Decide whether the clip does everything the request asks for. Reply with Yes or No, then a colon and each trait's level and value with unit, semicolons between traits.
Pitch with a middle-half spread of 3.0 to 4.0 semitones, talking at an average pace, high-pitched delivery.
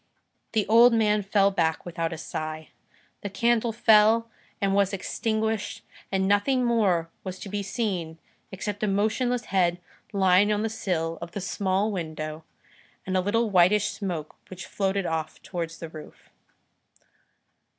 Yes: average, 3.7 semitones; average, 150 wpm; high, 195 Hz